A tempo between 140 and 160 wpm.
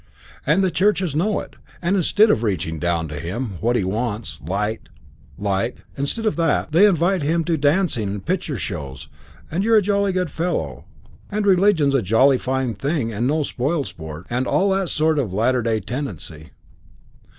No: average, 175 wpm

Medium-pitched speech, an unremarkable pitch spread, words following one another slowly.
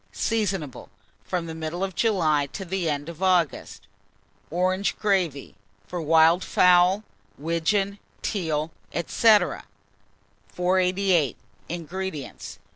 Yes: medium, 175 Hz; average, 3.6 semitones; slow, 95 wpm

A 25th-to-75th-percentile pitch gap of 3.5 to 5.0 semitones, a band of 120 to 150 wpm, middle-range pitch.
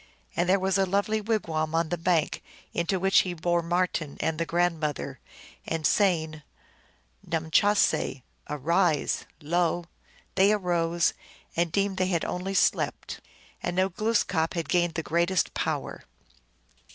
No: average, 2.8 semitones; average, 140 wpm; medium, 175 Hz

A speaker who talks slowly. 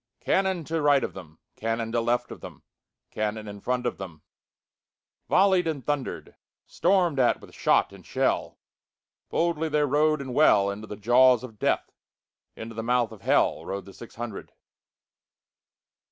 Yes: slow, 130 wpm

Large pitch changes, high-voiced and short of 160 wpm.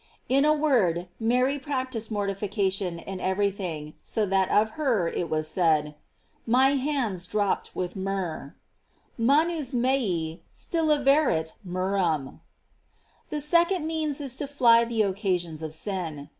Yes: wide, 7.3 semitones; high, 205 Hz; average, 150 wpm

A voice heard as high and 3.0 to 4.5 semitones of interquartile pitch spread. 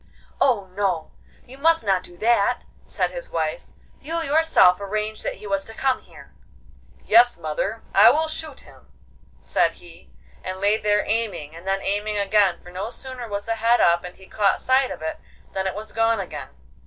Yes: high, 210 Hz; average, 4.1 semitones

